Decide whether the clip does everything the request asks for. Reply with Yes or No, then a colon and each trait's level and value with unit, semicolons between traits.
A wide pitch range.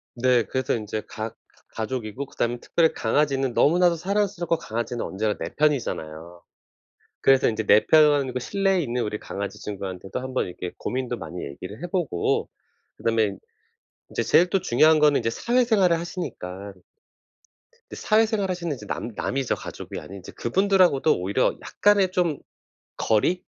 Yes: wide, 8.1 semitones